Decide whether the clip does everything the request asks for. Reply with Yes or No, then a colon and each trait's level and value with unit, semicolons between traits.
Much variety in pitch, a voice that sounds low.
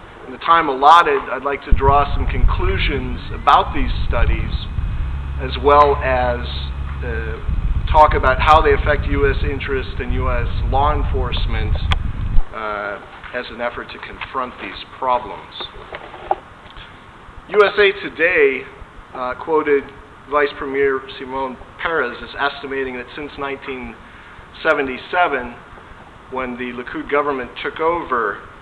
Yes: wide, 8.8 semitones; low, 130 Hz